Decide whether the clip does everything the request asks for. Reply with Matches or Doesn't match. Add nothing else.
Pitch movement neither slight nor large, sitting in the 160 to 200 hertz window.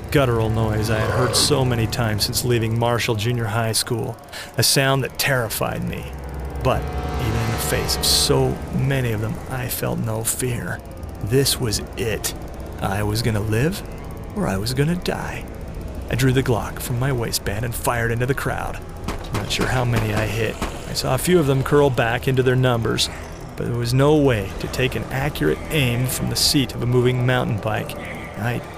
Doesn't match